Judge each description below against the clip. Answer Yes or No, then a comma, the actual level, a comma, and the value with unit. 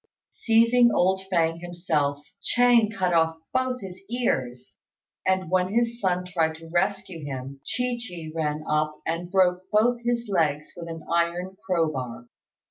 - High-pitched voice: No, medium, 175 Hz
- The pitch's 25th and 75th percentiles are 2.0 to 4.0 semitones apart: No, average, 4.9 semitones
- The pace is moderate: Yes, average, 145 wpm